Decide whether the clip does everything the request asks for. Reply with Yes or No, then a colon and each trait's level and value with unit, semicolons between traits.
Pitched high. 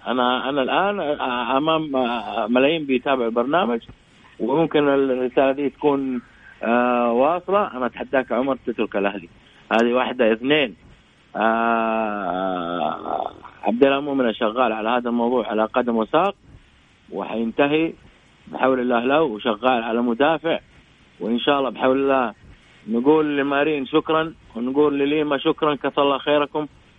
No: low, 130 Hz